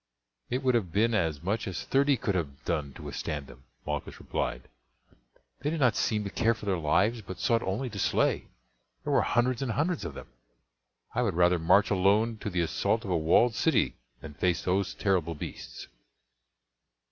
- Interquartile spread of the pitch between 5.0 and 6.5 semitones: Yes, average, 5.3 semitones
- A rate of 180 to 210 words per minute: Yes, average, 190 wpm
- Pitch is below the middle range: Yes, low, 100 Hz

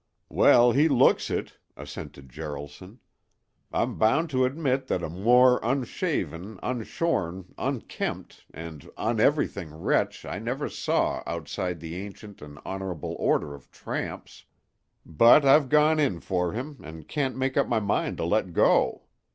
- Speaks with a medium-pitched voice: No, low, 105 Hz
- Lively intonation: Yes, wide, 7.8 semitones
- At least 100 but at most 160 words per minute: Yes, average, 140 wpm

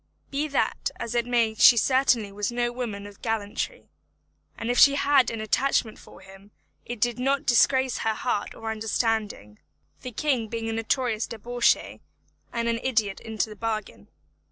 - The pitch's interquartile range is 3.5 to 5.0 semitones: No, narrow, 2.4 semitones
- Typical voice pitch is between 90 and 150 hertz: No, high, 230 Hz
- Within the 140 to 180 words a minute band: Yes, average, 170 wpm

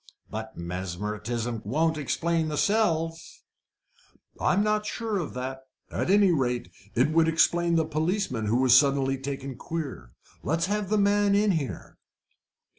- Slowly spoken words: No, average, 145 wpm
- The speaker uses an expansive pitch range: Yes, wide, 6.1 semitones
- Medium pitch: Yes, medium, 155 Hz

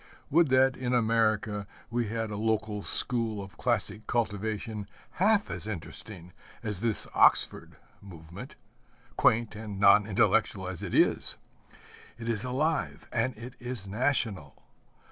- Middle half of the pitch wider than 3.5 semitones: No, average, 2.9 semitones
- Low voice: Yes, low, 110 Hz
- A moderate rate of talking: No, slow, 130 wpm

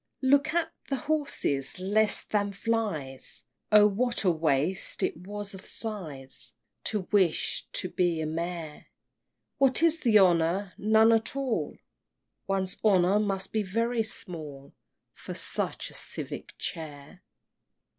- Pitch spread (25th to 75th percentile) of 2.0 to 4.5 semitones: No, average, 5.1 semitones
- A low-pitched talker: No, high, 195 Hz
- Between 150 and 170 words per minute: No, slow, 135 wpm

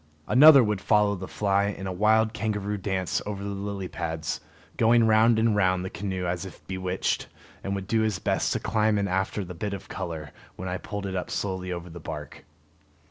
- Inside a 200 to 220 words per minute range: Yes, fast, 205 wpm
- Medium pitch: No, low, 100 Hz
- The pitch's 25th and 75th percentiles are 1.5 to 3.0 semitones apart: Yes, narrow, 2.4 semitones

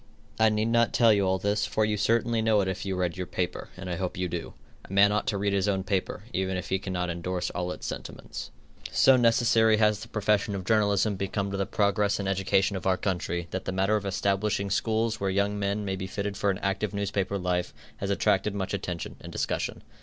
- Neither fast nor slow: No, fast, 230 wpm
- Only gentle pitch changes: Yes, narrow, 2.0 semitones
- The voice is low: Yes, low, 100 Hz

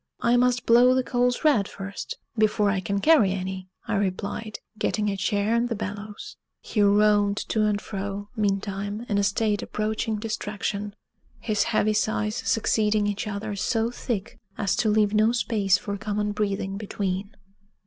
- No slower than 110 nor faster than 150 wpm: No, average, 160 wpm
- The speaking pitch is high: Yes, high, 210 Hz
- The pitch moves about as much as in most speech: No, narrow, 1.5 semitones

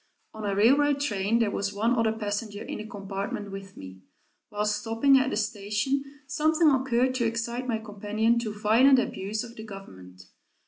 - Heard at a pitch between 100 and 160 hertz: No, high, 220 Hz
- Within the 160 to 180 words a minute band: Yes, average, 175 wpm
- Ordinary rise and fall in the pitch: Yes, average, 3.1 semitones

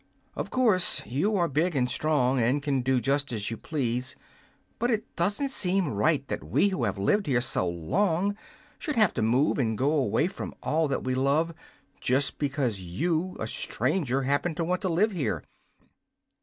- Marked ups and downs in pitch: Yes, wide, 6.0 semitones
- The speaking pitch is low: No, medium, 145 Hz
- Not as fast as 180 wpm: No, average, 185 wpm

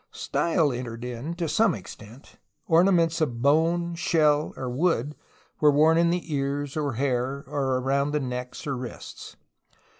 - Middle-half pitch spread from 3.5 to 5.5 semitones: Yes, average, 4.3 semitones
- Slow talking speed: No, average, 155 wpm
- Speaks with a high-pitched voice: No, medium, 145 Hz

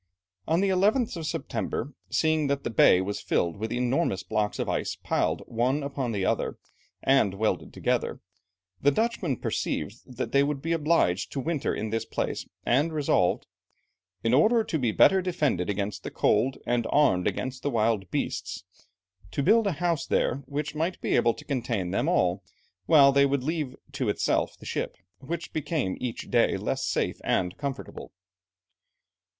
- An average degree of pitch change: No, wide, 6.0 semitones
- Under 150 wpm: No, average, 170 wpm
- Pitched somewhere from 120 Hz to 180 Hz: Yes, low, 135 Hz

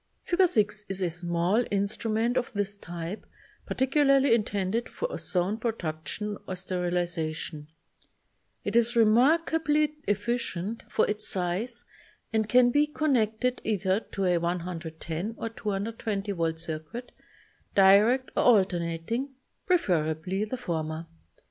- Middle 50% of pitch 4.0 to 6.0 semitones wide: Yes, average, 5.2 semitones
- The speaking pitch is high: Yes, high, 205 Hz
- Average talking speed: No, slow, 115 wpm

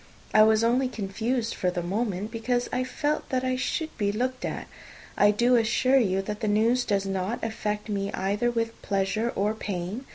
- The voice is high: Yes, high, 220 Hz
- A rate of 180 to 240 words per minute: Yes, average, 190 wpm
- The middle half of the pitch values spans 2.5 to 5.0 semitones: Yes, average, 3.4 semitones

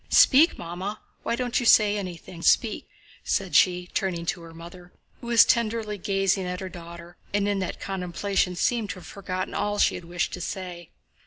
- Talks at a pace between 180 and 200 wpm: Yes, average, 185 wpm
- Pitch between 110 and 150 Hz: No, medium, 185 Hz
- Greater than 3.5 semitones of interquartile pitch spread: No, average, 2.8 semitones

